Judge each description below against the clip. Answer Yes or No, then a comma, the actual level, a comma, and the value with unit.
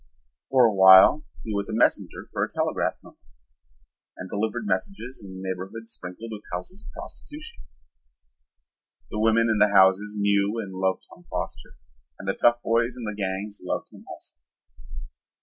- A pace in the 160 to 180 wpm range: Yes, average, 165 wpm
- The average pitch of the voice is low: Yes, low, 105 Hz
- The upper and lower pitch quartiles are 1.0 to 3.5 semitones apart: Yes, average, 3.2 semitones